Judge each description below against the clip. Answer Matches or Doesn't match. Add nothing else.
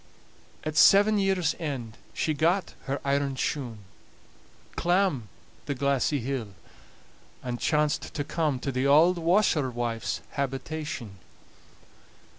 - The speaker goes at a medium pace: Doesn't match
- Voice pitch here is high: Doesn't match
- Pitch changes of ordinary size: Matches